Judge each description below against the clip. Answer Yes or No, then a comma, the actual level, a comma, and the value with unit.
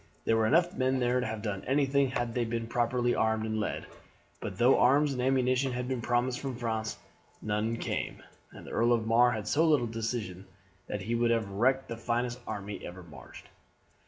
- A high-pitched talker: No, low, 120 Hz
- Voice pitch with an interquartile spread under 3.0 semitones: Yes, narrow, 2.4 semitones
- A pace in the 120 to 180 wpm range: No, fast, 205 wpm